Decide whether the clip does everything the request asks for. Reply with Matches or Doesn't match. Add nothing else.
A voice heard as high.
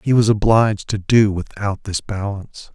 Doesn't match